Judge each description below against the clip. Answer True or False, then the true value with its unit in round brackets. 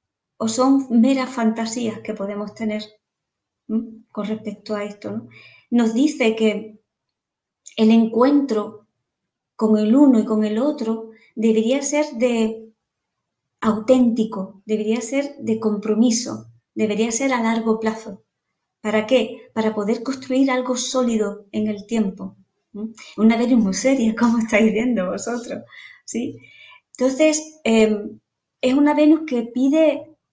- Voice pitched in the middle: False (225 Hz)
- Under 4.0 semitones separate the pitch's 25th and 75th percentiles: True (2.9 semitones)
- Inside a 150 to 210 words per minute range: False (130 wpm)